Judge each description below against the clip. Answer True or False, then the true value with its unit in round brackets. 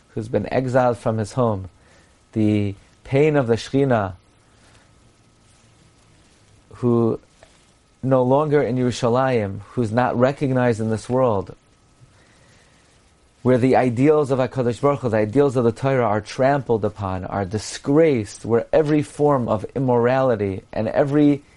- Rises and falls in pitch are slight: False (3.7 semitones)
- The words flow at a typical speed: False (120 wpm)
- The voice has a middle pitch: False (120 Hz)